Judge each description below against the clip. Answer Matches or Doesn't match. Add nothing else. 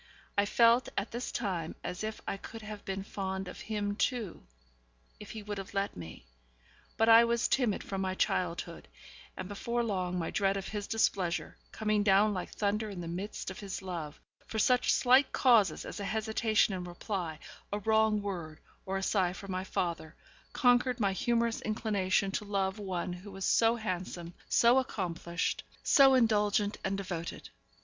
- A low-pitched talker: Doesn't match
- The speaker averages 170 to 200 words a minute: Matches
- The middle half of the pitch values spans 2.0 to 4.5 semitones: Matches